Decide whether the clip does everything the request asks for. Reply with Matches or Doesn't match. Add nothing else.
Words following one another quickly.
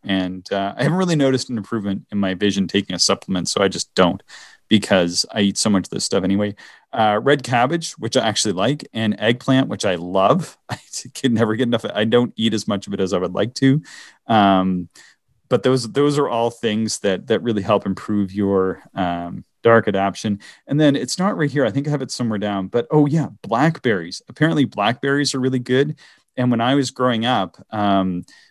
Matches